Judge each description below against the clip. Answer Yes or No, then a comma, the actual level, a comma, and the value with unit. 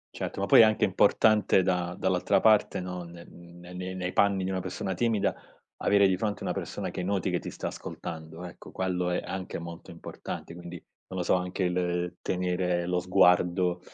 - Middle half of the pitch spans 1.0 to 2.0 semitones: Yes, narrow, 1.3 semitones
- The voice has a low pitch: Yes, very low, 90 Hz